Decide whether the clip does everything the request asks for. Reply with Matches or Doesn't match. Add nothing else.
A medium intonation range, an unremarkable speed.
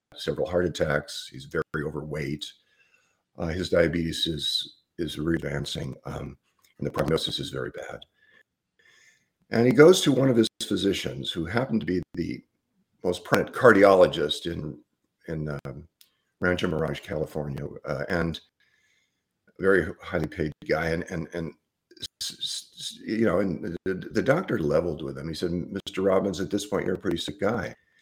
Doesn't match